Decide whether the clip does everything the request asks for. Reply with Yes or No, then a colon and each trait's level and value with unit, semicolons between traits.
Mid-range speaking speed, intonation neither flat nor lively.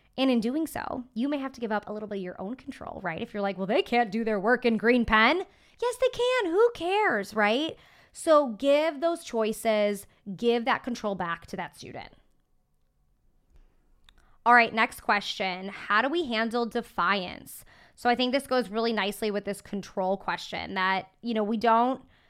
Yes: average, 195 wpm; average, 4.4 semitones